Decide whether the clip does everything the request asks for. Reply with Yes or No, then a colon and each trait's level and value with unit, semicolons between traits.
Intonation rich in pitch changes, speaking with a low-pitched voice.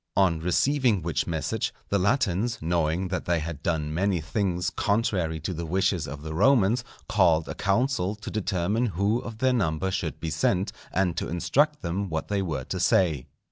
No: average, 4.1 semitones; very low, 90 Hz